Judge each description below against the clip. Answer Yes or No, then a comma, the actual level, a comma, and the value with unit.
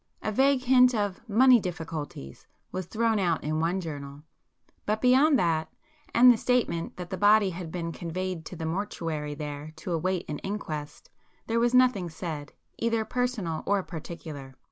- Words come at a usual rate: Yes, average, 160 wpm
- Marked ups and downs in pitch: Yes, wide, 5.9 semitones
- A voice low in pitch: No, medium, 180 Hz